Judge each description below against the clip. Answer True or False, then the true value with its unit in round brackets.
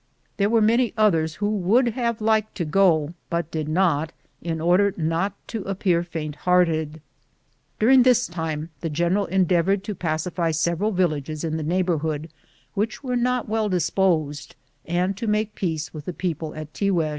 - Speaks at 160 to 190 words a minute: True (170 wpm)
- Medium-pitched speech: True (175 Hz)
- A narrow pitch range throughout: False (4.4 semitones)